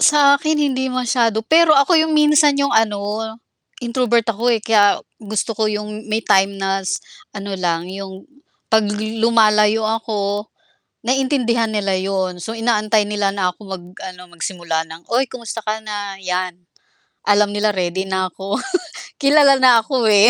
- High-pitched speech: Yes, high, 215 Hz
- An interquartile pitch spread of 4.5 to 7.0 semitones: No, average, 3.4 semitones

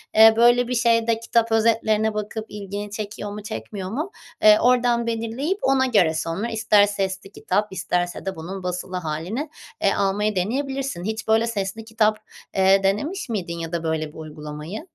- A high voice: Yes, high, 210 Hz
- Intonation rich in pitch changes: No, average, 3.5 semitones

